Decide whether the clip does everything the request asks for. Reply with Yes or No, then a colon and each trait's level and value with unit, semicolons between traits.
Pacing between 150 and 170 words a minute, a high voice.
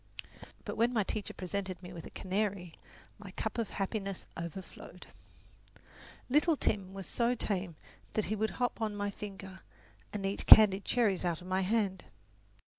Yes: average, 160 wpm; high, 200 Hz